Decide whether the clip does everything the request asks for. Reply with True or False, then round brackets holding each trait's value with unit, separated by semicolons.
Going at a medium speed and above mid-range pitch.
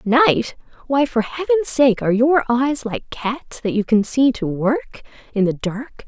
True (180 wpm; 245 Hz)